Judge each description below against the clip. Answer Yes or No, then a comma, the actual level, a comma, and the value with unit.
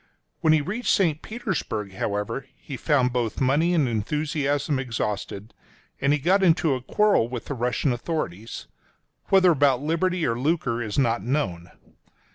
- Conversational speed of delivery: Yes, average, 155 wpm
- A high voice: No, medium, 140 Hz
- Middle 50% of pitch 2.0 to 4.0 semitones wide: No, wide, 5.5 semitones